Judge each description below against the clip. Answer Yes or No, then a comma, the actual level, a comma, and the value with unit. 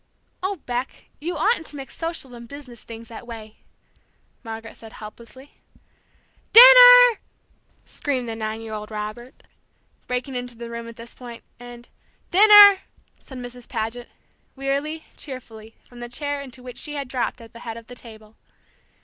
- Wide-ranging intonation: No, average, 3.8 semitones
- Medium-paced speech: Yes, average, 160 wpm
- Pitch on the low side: No, high, 245 Hz